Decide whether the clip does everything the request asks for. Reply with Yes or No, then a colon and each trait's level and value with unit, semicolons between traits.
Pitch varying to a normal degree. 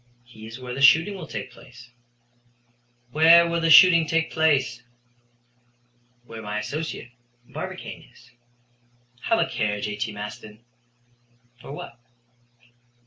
No: wide, 6.5 semitones